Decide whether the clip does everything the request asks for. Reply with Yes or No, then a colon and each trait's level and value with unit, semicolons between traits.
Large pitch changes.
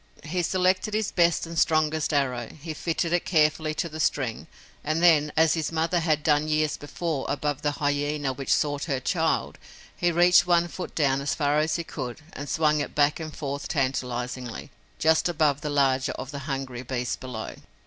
No: average, 2.8 semitones